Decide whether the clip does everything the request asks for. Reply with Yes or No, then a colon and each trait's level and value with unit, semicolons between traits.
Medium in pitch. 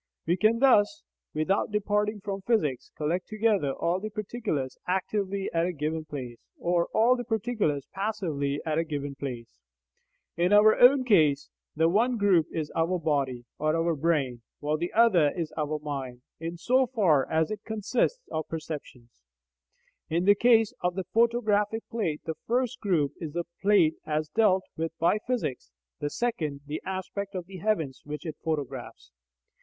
Yes: medium, 175 Hz